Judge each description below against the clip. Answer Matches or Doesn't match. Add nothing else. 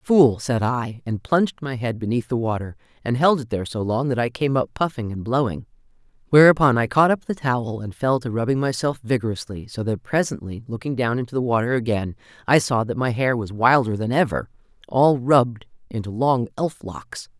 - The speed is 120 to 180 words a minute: Doesn't match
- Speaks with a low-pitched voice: Matches